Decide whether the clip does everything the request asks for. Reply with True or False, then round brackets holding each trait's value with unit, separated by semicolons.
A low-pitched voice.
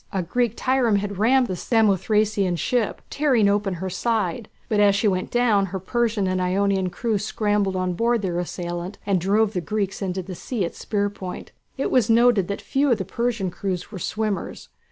False (200 Hz)